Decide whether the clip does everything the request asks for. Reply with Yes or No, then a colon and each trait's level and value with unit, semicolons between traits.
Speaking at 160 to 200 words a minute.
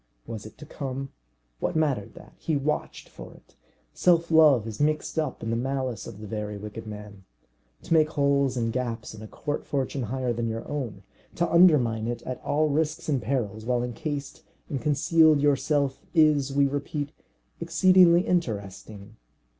Yes: average, 170 wpm